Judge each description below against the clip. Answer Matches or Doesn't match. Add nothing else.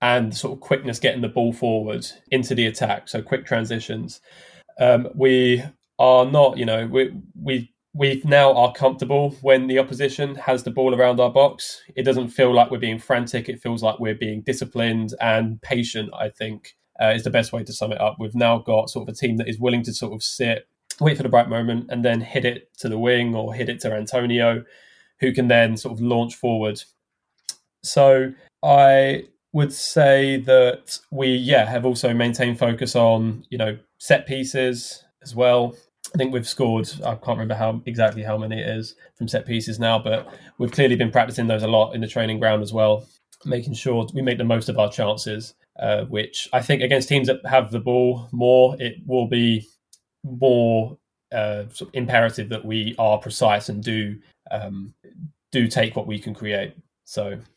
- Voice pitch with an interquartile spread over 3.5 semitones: Doesn't match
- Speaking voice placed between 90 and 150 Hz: Matches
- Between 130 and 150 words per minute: Doesn't match